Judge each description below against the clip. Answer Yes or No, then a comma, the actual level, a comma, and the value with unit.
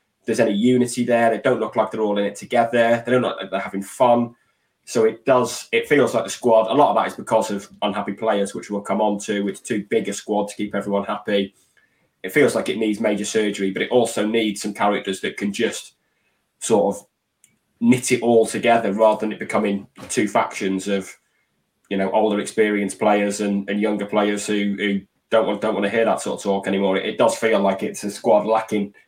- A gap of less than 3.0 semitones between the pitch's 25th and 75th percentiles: Yes, narrow, 2.4 semitones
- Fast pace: Yes, fast, 230 wpm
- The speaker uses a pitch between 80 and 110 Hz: Yes, low, 105 Hz